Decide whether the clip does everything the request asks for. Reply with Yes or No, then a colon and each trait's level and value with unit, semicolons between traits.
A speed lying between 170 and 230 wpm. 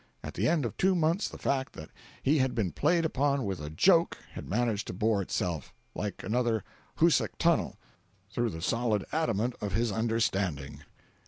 Yes: average, 175 wpm